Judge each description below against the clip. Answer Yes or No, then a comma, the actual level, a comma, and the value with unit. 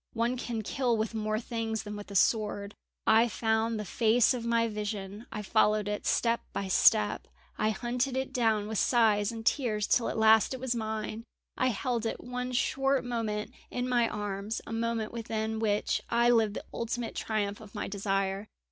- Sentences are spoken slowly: No, average, 185 wpm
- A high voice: Yes, high, 220 Hz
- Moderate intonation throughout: No, narrow, 2.1 semitones